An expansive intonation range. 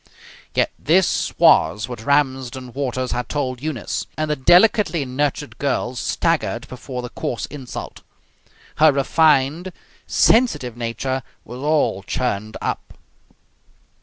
No: average, 3.5 semitones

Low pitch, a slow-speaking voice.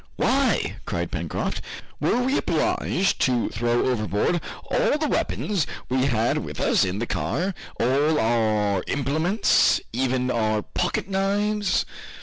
Yes: low, 130 Hz; slow, 130 wpm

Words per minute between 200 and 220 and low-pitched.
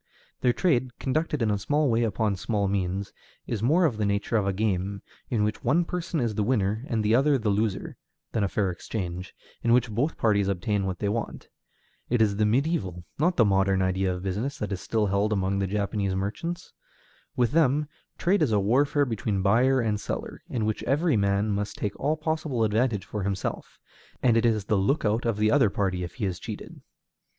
Yes: fast, 205 wpm; low, 110 Hz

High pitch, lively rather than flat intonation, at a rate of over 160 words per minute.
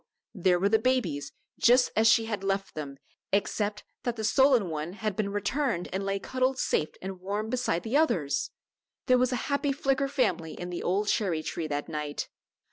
Yes: high, 205 Hz; wide, 6.1 semitones; average, 190 wpm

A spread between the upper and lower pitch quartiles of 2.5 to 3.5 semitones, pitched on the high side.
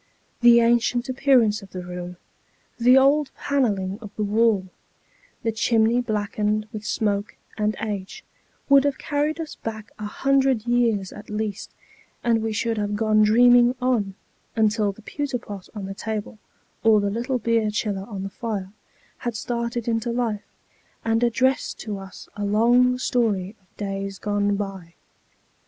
Yes: average, 2.9 semitones; high, 220 Hz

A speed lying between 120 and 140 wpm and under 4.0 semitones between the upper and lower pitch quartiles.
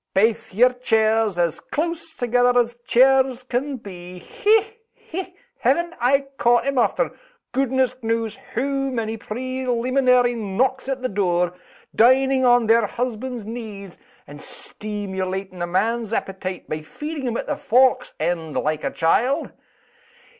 No: slow, 135 wpm; average, 4.3 semitones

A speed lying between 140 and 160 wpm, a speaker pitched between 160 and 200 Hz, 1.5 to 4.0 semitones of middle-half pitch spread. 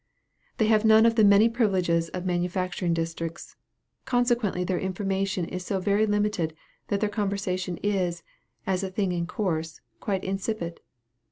Yes: average, 150 wpm; high, 190 Hz; average, 2.7 semitones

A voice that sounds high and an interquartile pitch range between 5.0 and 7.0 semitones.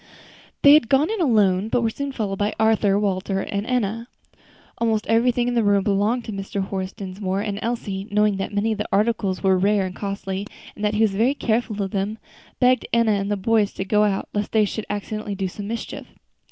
No: high, 210 Hz; narrow, 2.5 semitones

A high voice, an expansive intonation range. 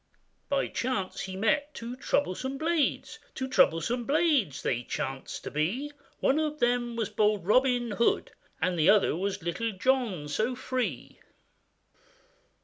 Yes: high, 235 Hz; wide, 5.7 semitones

